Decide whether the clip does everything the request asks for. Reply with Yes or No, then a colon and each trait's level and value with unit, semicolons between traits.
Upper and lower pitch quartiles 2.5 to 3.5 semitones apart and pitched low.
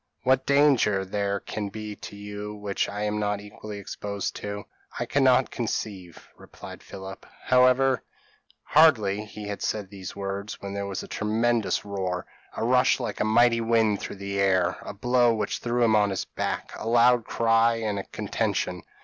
Yes: average, 2.8 semitones; low, 105 Hz